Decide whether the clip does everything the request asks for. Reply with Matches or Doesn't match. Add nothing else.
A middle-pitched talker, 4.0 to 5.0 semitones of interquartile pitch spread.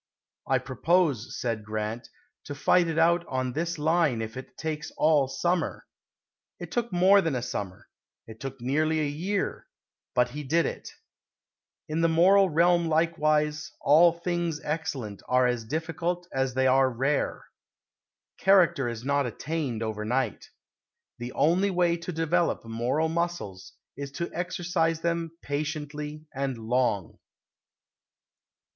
Matches